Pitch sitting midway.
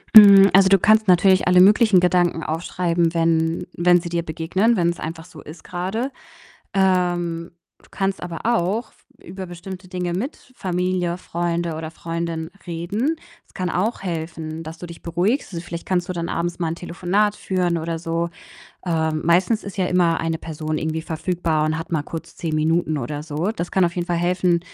Yes: medium, 175 Hz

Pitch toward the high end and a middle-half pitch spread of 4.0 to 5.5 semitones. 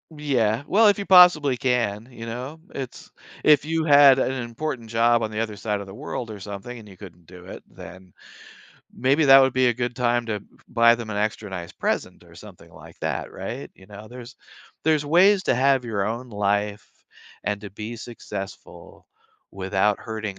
No: low, 115 Hz; average, 4.3 semitones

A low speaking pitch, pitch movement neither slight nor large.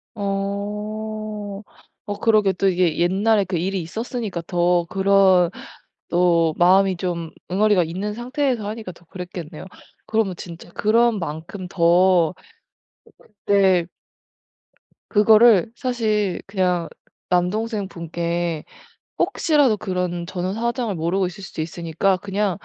No: high, 190 Hz; average, 3.4 semitones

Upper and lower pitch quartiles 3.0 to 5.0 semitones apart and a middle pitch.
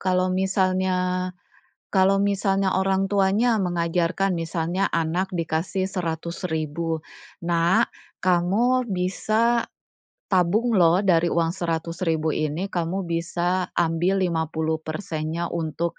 No: narrow, 2.5 semitones; medium, 180 Hz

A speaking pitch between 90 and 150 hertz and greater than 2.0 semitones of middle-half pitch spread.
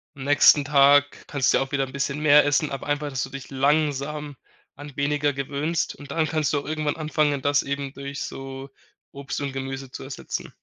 No: medium, 140 Hz; narrow, 1.3 semitones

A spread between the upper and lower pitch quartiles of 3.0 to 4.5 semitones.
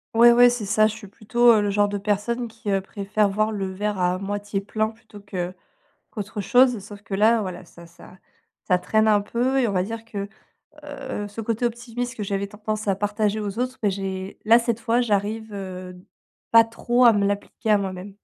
No: narrow, 2.4 semitones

